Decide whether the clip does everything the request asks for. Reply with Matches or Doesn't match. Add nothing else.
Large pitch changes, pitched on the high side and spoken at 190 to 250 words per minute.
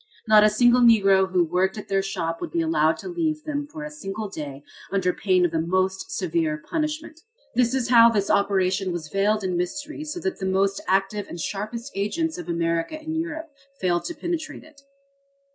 Matches